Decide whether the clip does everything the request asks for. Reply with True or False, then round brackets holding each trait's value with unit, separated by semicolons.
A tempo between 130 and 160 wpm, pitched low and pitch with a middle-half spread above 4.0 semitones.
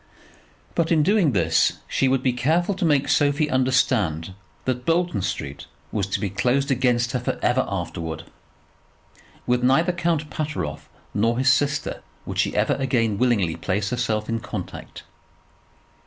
True (150 wpm; 125 Hz; 5.5 semitones)